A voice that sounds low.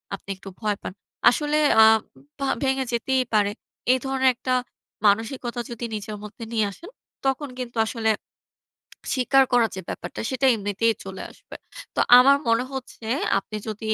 No: high, 235 Hz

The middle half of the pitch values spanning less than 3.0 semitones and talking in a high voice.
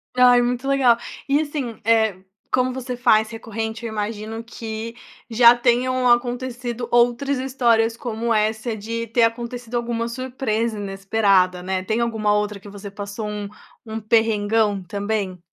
Yes: narrow, 2.4 semitones; high, 230 Hz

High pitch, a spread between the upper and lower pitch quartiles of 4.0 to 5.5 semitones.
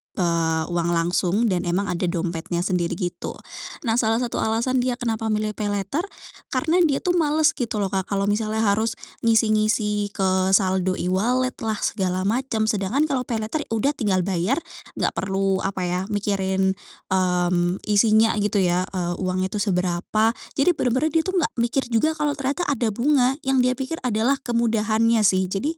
Yes: high, 210 Hz; average, 4.6 semitones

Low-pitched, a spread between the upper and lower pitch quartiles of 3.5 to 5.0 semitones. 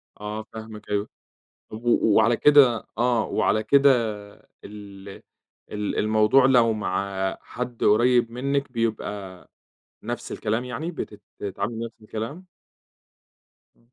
No: low, 110 Hz; average, 2.9 semitones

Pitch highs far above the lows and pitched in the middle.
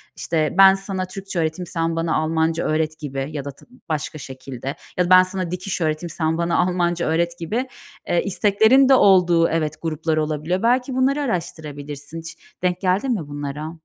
No: average, 3.2 semitones; medium, 165 Hz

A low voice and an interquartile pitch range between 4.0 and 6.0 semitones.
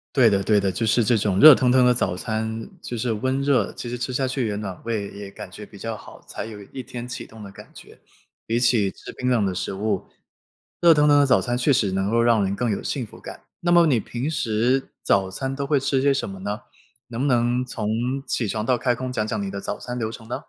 No: low, 115 Hz; average, 3.6 semitones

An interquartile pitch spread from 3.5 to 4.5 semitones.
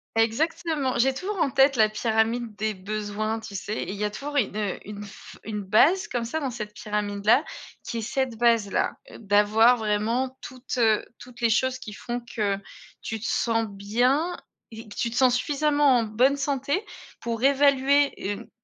Yes: average, 3.8 semitones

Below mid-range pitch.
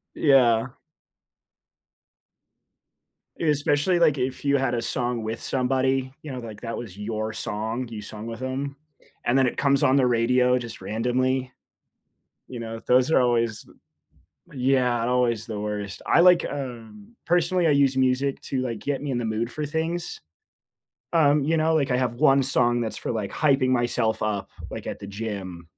Yes: low, 125 Hz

